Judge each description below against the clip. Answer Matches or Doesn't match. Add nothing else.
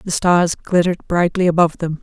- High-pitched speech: Doesn't match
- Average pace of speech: Matches